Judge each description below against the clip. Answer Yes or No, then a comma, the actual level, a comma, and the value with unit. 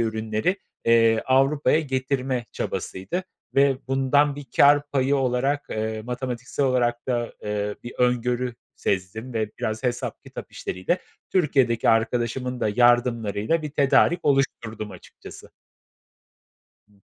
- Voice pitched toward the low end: Yes, low, 125 Hz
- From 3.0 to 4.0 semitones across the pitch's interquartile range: Yes, average, 3.3 semitones